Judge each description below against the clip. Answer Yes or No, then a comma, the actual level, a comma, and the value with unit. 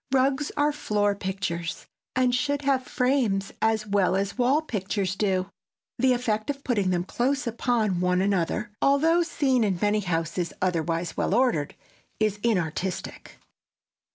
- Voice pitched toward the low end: No, high, 210 Hz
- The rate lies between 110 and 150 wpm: Yes, average, 140 wpm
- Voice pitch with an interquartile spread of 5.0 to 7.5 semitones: Yes, wide, 5.6 semitones